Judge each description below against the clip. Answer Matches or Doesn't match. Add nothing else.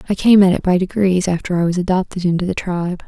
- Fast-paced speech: Matches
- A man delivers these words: Doesn't match